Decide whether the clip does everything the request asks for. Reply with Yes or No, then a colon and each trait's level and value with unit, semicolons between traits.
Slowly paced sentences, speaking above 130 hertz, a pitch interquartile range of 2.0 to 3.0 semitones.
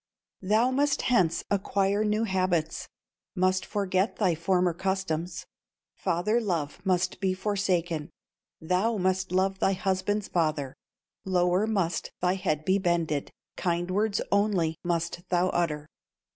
Yes: slow, 125 wpm; medium, 185 Hz; narrow, 2.5 semitones